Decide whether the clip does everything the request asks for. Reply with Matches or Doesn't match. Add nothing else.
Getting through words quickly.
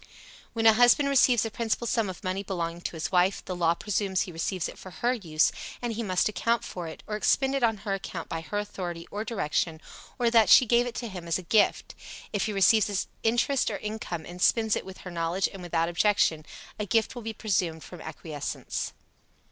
Matches